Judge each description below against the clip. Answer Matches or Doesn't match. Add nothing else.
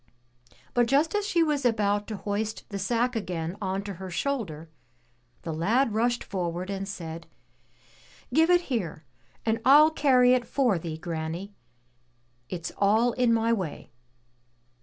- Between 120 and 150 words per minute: Matches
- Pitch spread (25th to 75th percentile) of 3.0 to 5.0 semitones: Doesn't match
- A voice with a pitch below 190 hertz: Doesn't match